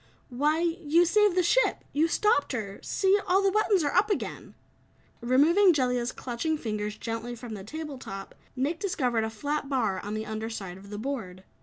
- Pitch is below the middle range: No, very high, 265 Hz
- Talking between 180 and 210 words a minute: Yes, average, 185 wpm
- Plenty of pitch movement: Yes, wide, 7.3 semitones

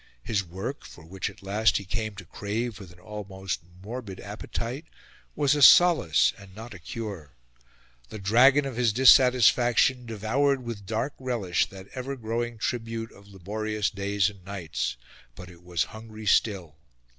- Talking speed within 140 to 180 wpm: Yes, average, 155 wpm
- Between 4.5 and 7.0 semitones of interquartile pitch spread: No, average, 3.8 semitones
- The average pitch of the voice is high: No, low, 110 Hz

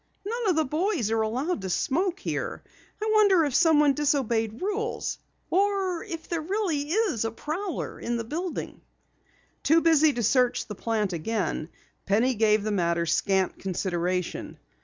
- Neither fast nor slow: Yes, average, 150 wpm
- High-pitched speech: Yes, very high, 280 Hz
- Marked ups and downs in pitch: Yes, wide, 8.7 semitones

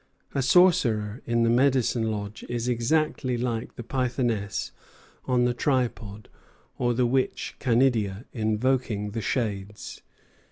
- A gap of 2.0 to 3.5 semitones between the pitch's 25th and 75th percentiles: Yes, average, 2.9 semitones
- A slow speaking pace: Yes, slow, 120 wpm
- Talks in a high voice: No, low, 120 Hz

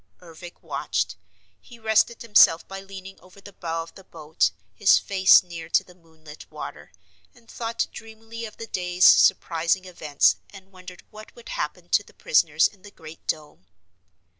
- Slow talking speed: No, average, 165 wpm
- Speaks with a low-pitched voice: No, medium, 185 Hz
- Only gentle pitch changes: No, average, 4.5 semitones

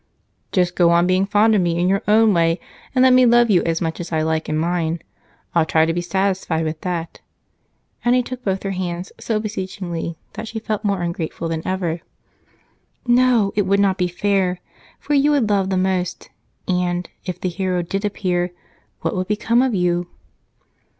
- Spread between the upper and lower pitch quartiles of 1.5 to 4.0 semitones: Yes, average, 3.3 semitones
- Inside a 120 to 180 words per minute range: No, average, 195 wpm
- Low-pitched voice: No, medium, 185 Hz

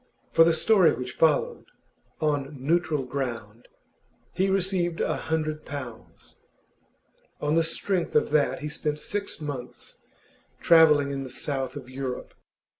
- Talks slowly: Yes, slow, 130 wpm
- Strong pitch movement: No, average, 3.3 semitones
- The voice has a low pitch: No, medium, 150 Hz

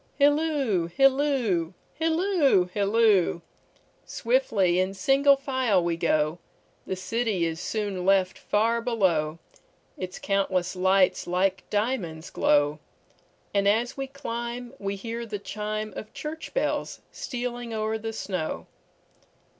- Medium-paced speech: No, slow, 100 wpm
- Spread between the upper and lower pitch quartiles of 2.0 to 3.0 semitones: No, average, 5.3 semitones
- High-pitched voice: Yes, high, 210 Hz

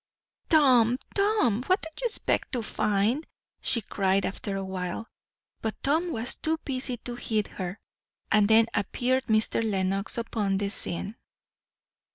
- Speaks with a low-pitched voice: No, high, 225 Hz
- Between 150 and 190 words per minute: No, average, 140 wpm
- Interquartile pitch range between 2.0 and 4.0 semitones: No, average, 4.5 semitones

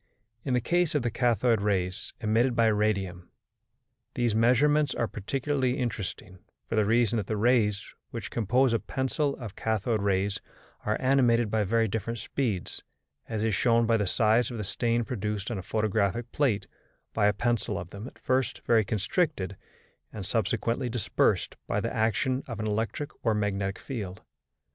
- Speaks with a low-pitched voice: Yes, low, 115 Hz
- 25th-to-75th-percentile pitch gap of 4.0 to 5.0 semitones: No, average, 2.9 semitones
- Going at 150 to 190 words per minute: Yes, average, 165 wpm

